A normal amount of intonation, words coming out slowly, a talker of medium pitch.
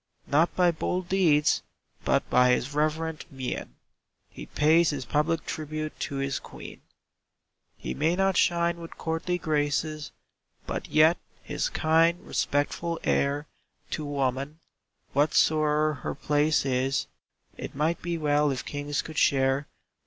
No: narrow, 2.3 semitones; slow, 130 wpm; medium, 150 Hz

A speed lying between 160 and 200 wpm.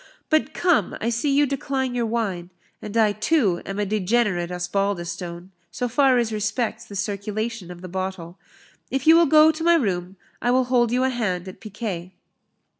Yes: average, 185 wpm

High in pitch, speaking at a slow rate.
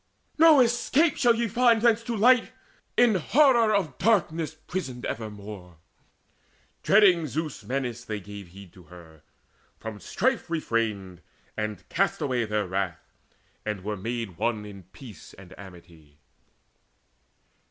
No: low, 120 Hz; slow, 130 wpm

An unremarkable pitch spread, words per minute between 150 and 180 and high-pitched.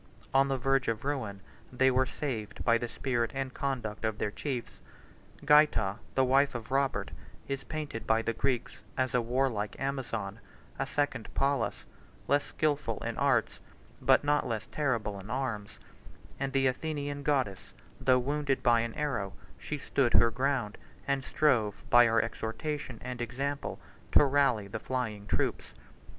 No: average, 3.4 semitones; average, 160 wpm; low, 130 Hz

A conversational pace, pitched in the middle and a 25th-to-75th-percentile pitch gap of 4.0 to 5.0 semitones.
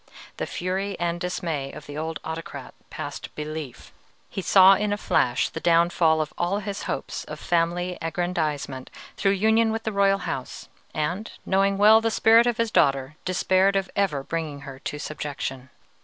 Yes: average, 170 wpm; medium, 175 Hz; average, 4.5 semitones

